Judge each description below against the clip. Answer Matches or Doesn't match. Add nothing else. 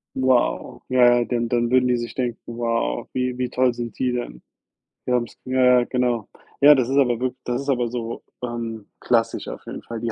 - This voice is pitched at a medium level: Doesn't match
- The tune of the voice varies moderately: Doesn't match